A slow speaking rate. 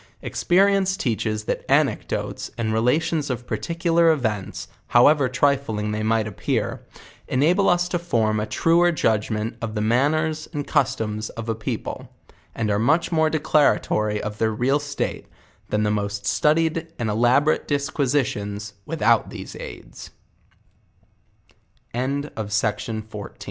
Yes: slow, 120 wpm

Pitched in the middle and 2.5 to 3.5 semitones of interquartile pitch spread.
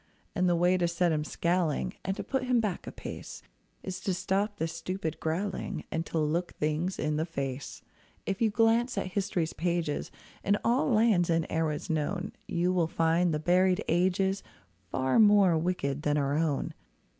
Yes: medium, 175 Hz; average, 3.2 semitones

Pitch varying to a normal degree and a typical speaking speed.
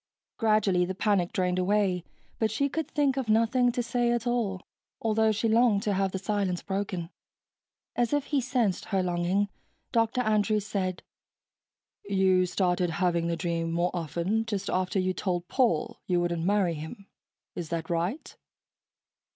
Yes: average, 4.0 semitones; average, 160 wpm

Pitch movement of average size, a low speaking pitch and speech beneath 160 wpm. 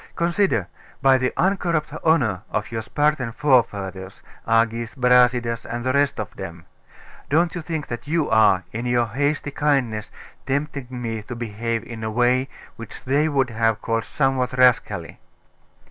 Yes: average, 4.0 semitones; low, 125 Hz; average, 150 wpm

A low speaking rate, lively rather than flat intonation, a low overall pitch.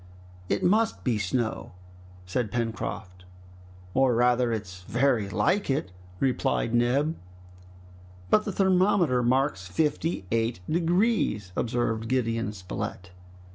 Yes: slow, 105 wpm; wide, 5.7 semitones; low, 120 Hz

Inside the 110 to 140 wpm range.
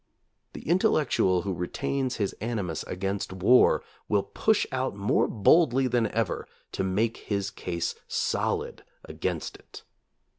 Yes: slow, 135 wpm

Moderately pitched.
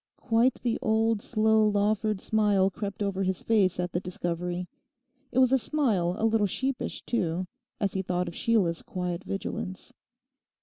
No: high, 200 Hz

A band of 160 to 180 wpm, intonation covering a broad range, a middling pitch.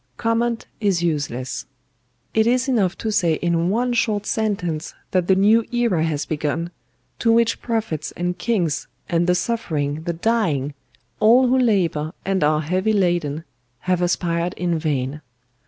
No: average, 150 wpm; wide, 5.7 semitones; medium, 180 Hz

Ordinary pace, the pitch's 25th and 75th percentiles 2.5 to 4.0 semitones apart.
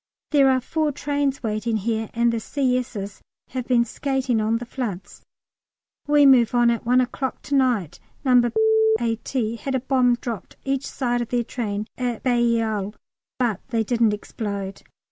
Yes: average, 160 wpm; average, 2.8 semitones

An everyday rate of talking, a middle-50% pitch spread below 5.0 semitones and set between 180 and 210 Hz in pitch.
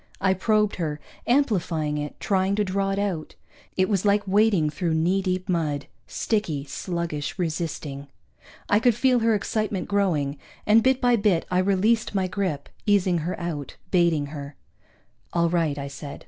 Yes: average, 160 wpm; average, 4.6 semitones; medium, 185 Hz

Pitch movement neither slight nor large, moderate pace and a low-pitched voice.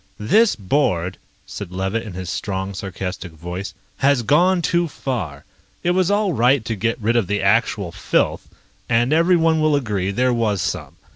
No: wide, 7.6 semitones; average, 165 wpm; low, 115 Hz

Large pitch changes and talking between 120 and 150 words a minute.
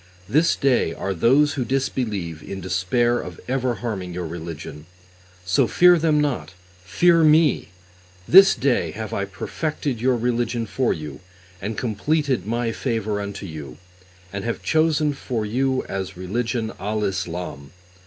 Yes: wide, 6.1 semitones; average, 145 wpm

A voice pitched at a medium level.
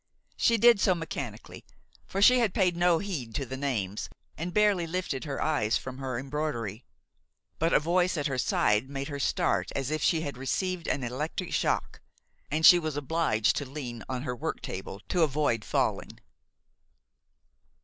Yes: medium, 145 Hz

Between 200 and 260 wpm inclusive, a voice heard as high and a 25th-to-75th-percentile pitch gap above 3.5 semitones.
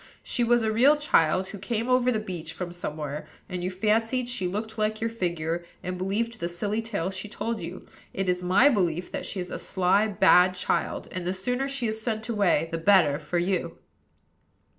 Yes: fast, 205 wpm; high, 195 Hz; average, 4.0 semitones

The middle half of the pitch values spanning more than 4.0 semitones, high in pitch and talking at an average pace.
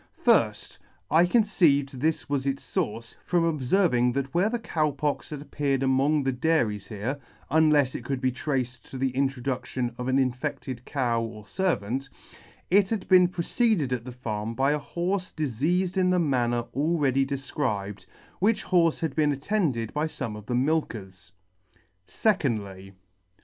No: average, 4.7 semitones; medium, 140 Hz; average, 160 wpm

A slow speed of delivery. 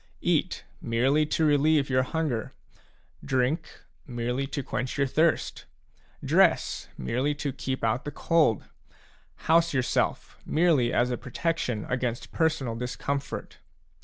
Yes: slow, 120 wpm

